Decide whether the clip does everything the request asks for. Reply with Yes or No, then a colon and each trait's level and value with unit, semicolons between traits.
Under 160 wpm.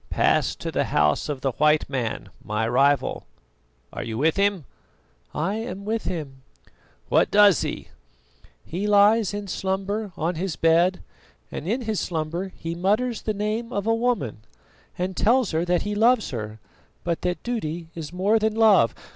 No: average, 165 wpm